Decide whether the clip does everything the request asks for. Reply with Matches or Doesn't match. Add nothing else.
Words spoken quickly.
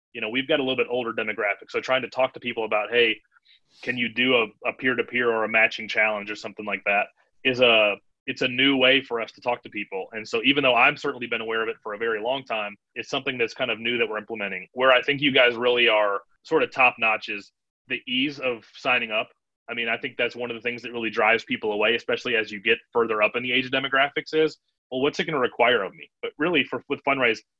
Matches